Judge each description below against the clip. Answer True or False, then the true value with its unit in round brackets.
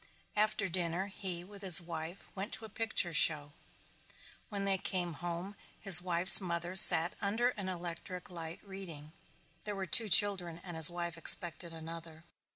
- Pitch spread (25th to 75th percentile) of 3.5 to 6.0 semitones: False (2.7 semitones)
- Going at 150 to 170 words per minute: True (160 wpm)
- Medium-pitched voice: True (180 Hz)